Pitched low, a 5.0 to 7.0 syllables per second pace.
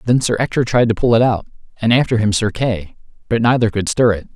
Yes: low, 110 Hz; 6.0 syllables/s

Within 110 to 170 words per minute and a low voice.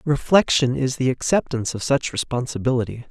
Yes: slow, 135 wpm; low, 130 Hz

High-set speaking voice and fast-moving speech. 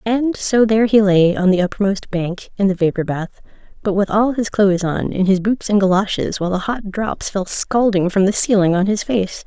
Yes: high, 200 Hz; fast, 230 wpm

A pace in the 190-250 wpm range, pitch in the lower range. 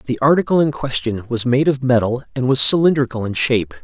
Yes: fast, 205 wpm; low, 130 Hz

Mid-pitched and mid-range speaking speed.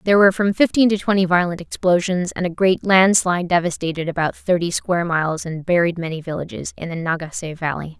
Yes: medium, 175 Hz; average, 190 wpm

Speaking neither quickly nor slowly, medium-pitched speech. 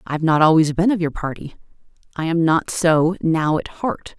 No: fast, 215 wpm; medium, 165 Hz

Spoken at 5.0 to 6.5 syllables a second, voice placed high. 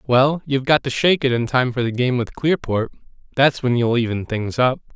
No: 5.4 syllables/s; low, 125 Hz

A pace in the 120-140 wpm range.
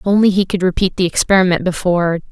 No: fast, 205 wpm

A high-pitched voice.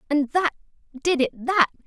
Yes: very high, 295 Hz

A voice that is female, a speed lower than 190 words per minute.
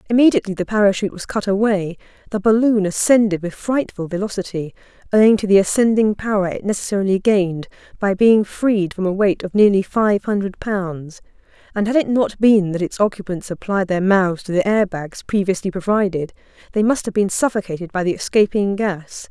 Yes: female; average, 175 wpm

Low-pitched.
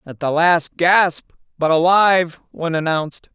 No: medium, 165 Hz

